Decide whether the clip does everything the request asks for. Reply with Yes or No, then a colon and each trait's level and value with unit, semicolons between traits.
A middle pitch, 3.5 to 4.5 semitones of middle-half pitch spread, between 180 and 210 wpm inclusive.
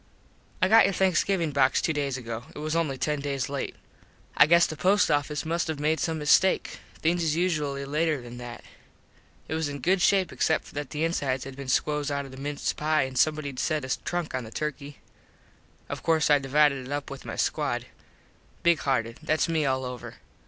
No: medium, 150 Hz; average, 2.8 semitones; fast, 205 wpm